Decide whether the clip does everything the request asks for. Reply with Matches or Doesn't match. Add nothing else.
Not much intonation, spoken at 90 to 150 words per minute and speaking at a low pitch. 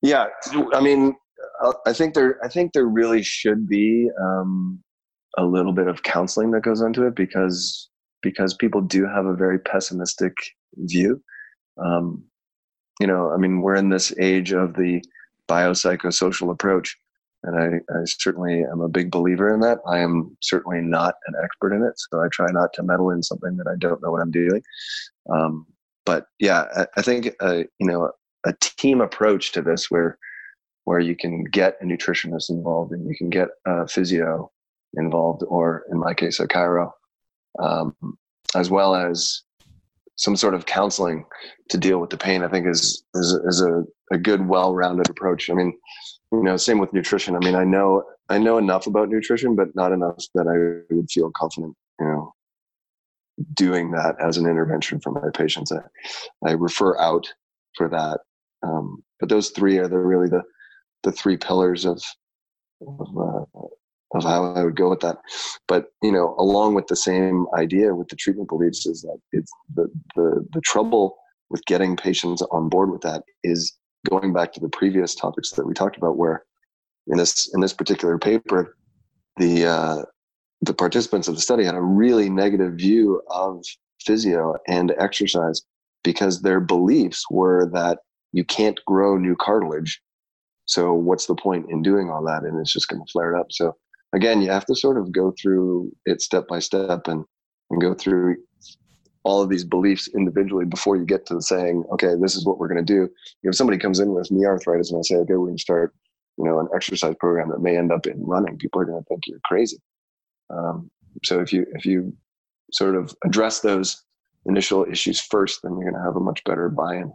Doesn't match